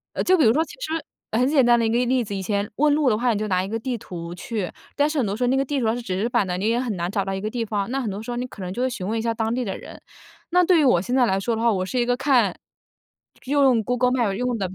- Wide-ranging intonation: No, average, 4.0 semitones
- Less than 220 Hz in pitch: No, high, 235 Hz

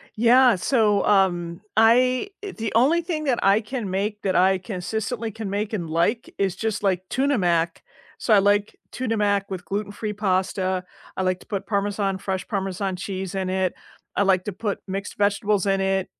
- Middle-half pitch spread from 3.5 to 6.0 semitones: No, average, 2.7 semitones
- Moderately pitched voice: No, high, 200 Hz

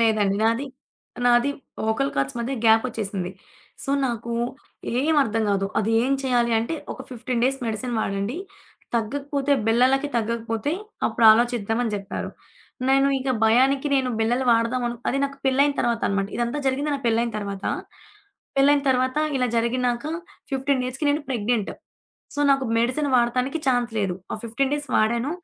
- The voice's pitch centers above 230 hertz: Yes, high, 240 Hz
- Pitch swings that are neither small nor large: Yes, average, 3.2 semitones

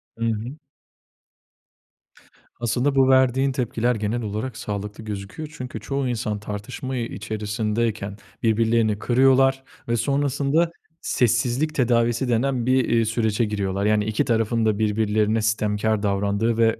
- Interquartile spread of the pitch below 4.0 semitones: Yes, average, 3.1 semitones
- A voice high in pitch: No, low, 115 Hz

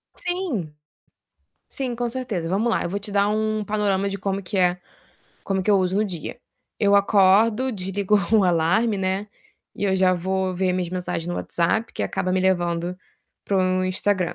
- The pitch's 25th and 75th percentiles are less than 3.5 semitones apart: Yes, narrow, 2.4 semitones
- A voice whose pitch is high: Yes, high, 195 Hz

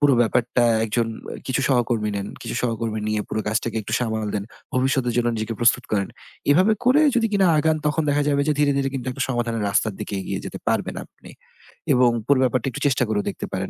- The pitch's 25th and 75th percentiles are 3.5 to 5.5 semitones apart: Yes, average, 4.2 semitones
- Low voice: Yes, low, 120 Hz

